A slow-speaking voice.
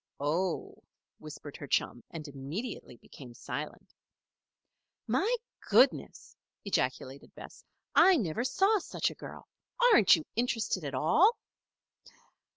Yes: slow, 110 wpm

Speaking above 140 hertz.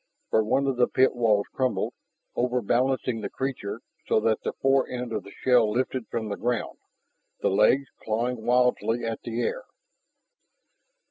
No: low, 120 Hz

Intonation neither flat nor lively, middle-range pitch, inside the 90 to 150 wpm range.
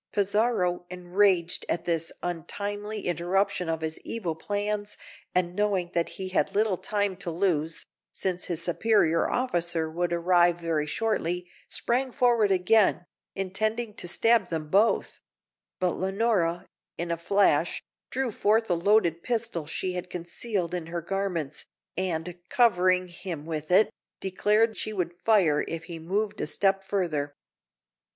Yes: average, 3.4 semitones; medium, 180 Hz; average, 140 wpm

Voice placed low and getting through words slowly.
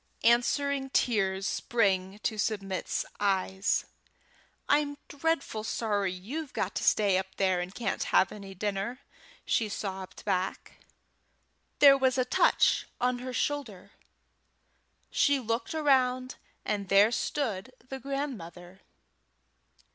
No: high, 220 Hz; slow, 115 wpm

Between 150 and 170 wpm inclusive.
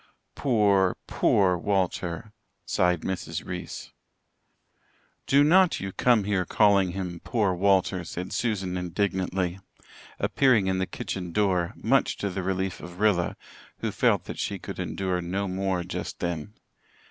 No: slow, 135 wpm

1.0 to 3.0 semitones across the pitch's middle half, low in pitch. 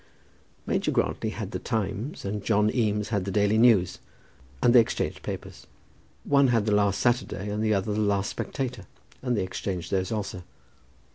Yes: average, 2.7 semitones; low, 105 Hz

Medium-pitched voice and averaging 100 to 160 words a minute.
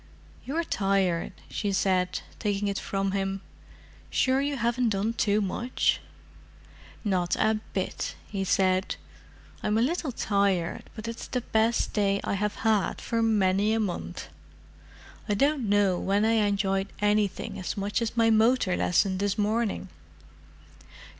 No: high, 205 Hz; average, 140 wpm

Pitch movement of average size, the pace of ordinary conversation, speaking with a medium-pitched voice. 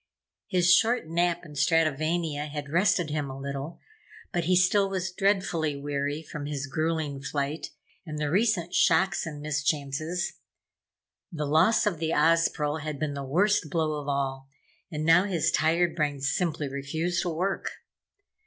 Yes: average, 3.3 semitones; average, 155 wpm; medium, 160 Hz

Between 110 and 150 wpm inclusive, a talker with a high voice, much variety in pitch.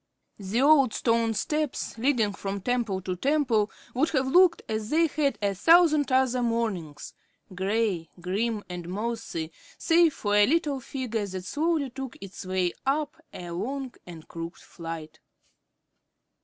Yes: average, 140 wpm; high, 230 Hz; wide, 6.6 semitones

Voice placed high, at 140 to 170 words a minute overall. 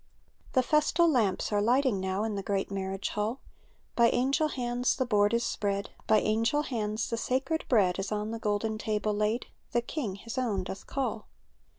No: high, 220 Hz; average, 185 wpm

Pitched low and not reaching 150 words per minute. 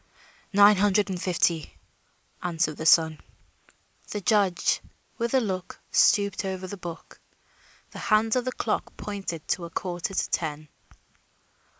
No: high, 190 Hz; average, 140 wpm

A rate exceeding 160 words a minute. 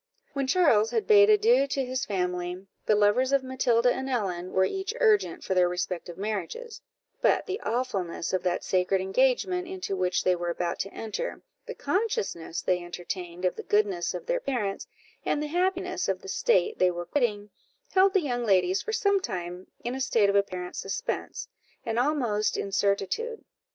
Yes: average, 175 wpm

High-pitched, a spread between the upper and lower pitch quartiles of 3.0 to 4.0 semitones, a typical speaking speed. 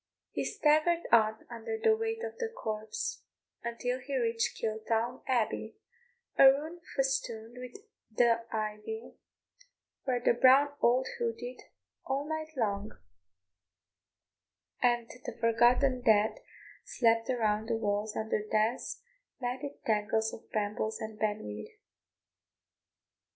No: high, 235 Hz; average, 3.6 semitones; slow, 115 wpm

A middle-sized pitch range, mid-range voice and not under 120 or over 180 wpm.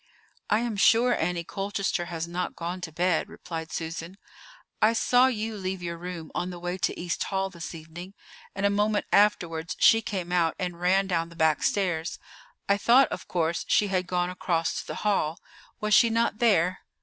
No: average, 3.1 semitones; medium, 180 Hz; average, 190 wpm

